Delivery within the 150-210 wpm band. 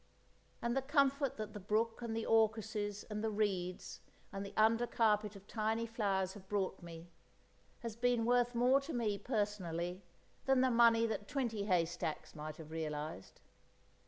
Yes: average, 160 wpm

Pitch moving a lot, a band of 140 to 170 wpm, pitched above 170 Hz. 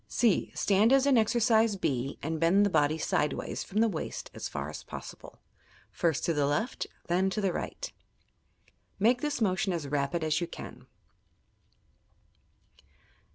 Yes: wide, 6.1 semitones; average, 160 wpm; medium, 185 Hz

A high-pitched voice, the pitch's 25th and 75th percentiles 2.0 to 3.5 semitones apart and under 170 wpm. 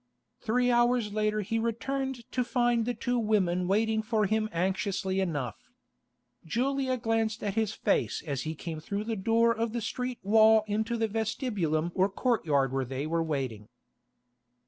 No: high, 215 Hz; average, 4.5 semitones; average, 160 wpm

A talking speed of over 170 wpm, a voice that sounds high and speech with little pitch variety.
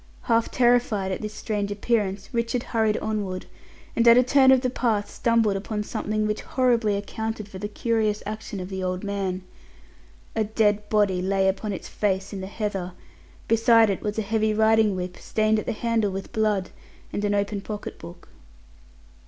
Yes: average, 180 wpm; high, 210 Hz; narrow, 2.2 semitones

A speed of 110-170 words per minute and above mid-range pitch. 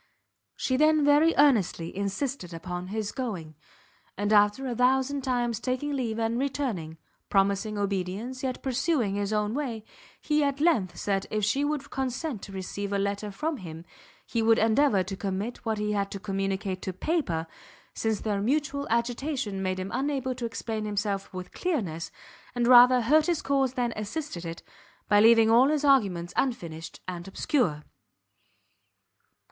Yes: average, 160 wpm; high, 225 Hz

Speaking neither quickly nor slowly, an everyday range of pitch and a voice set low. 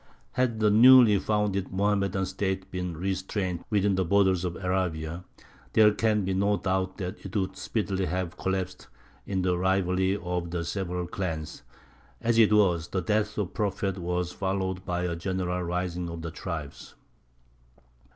No: average, 160 wpm; narrow, 2.1 semitones; very low, 95 Hz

